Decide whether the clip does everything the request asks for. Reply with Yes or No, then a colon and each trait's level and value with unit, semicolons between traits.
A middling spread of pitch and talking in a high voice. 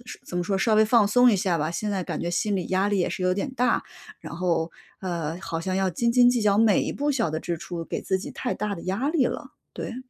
Yes: average, 4.8 semitones; high, 195 Hz